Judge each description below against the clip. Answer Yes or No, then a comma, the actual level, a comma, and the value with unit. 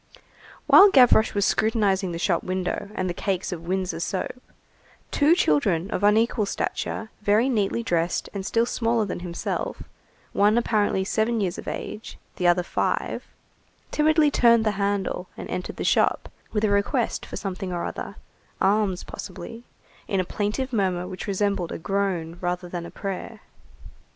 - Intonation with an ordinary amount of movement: Yes, average, 3.5 semitones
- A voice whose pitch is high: Yes, high, 200 Hz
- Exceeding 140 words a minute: Yes, average, 160 wpm